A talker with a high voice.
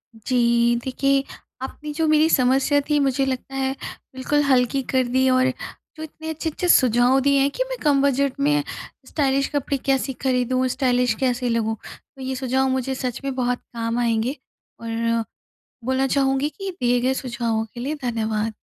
Yes: very high, 260 Hz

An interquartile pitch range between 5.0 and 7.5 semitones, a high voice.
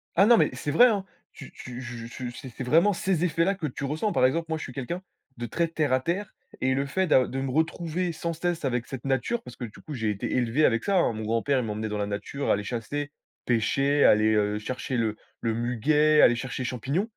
No: wide, 5.4 semitones; low, 135 Hz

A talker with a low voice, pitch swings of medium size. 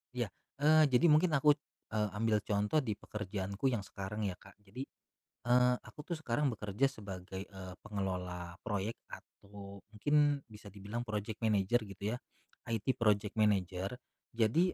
Yes: low, 105 Hz; average, 3.8 semitones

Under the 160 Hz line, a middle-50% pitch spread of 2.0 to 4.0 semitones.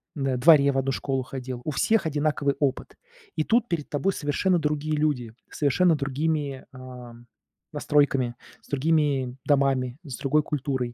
Yes: medium, 140 Hz; average, 2.7 semitones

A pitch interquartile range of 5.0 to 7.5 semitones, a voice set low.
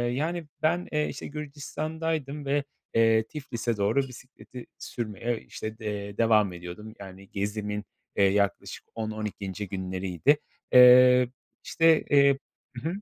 Yes: wide, 5.6 semitones; low, 115 Hz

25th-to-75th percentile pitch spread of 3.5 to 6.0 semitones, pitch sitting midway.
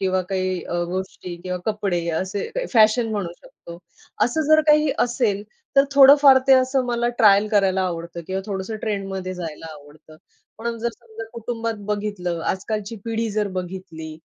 No: average, 4.0 semitones; high, 205 Hz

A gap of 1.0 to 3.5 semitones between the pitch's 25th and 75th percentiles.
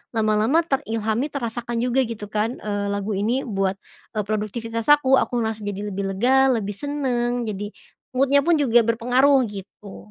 No: average, 4.0 semitones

